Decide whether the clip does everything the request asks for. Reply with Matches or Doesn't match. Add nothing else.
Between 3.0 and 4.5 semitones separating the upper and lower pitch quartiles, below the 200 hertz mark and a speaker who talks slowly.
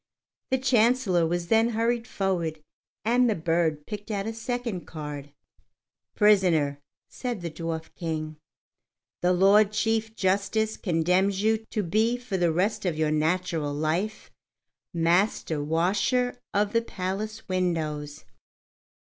Doesn't match